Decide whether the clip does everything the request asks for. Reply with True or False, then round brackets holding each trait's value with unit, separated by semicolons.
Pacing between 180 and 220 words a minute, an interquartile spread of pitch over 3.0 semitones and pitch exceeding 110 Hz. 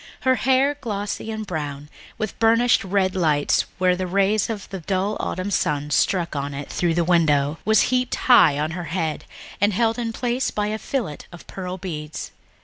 True (185 wpm; 5.4 semitones; 190 Hz)